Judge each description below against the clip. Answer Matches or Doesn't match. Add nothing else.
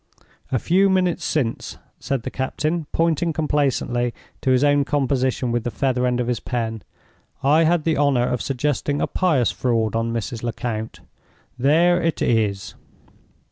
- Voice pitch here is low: Matches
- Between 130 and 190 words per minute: Matches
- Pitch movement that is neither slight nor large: Matches